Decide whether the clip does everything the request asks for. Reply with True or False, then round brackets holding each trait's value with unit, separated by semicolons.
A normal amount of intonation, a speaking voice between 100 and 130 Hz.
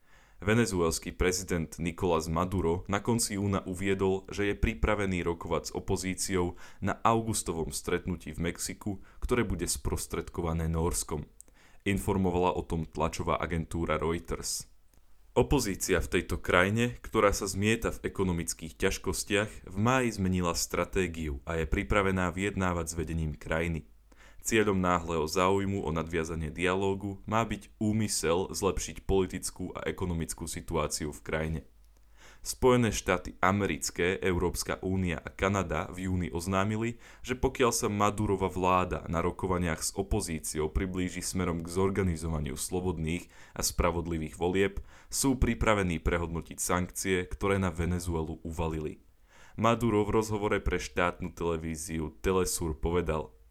False (3.2 semitones; 90 Hz)